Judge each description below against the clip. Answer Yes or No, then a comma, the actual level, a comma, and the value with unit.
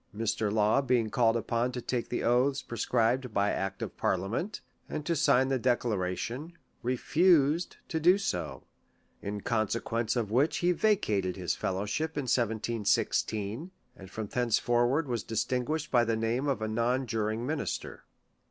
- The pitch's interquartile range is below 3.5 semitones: No, average, 3.9 semitones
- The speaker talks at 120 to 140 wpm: No, average, 160 wpm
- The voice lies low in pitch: Yes, low, 120 Hz